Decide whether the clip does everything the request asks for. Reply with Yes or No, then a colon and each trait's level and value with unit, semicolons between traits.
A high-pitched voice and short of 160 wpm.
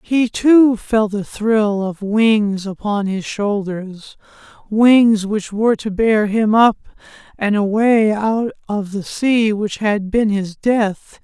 Yes: high, 210 Hz; average, 150 wpm